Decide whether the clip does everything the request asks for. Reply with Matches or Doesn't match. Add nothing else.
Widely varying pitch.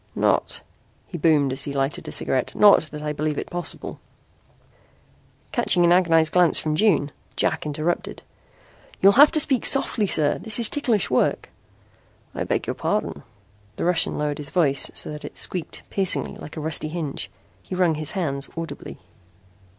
Doesn't match